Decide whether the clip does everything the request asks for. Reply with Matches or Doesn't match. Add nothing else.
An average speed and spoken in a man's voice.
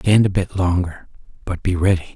Matches